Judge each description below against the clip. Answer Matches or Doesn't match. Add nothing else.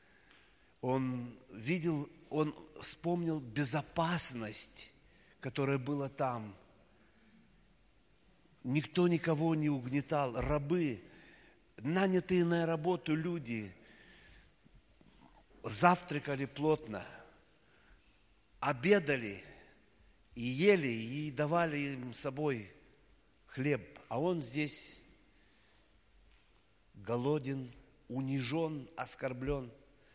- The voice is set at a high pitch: Doesn't match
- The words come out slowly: Matches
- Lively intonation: Doesn't match